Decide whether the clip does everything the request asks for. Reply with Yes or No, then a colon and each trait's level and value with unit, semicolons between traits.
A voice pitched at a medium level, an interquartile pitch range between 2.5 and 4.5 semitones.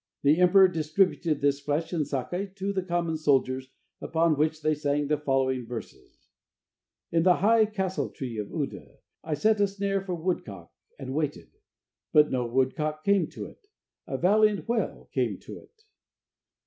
No: medium, 160 Hz; average, 5.1 semitones